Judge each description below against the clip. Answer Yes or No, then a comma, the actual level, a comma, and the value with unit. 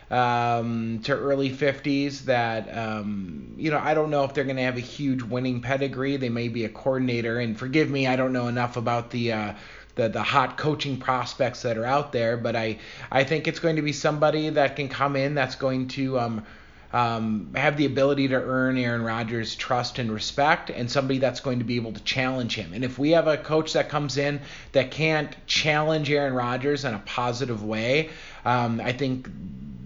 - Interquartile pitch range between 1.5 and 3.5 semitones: Yes, average, 3.1 semitones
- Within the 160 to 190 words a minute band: No, fast, 205 wpm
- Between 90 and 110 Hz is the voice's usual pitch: No, low, 130 Hz